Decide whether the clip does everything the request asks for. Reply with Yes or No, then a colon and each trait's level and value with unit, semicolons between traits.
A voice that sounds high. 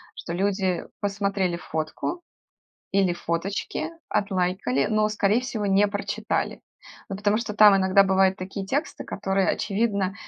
Yes: high, 195 Hz